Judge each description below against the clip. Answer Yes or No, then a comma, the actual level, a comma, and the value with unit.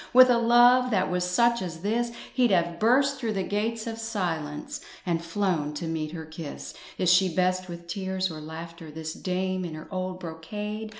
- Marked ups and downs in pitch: No, average, 4.9 semitones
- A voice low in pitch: No, medium, 185 Hz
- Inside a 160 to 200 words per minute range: Yes, average, 190 wpm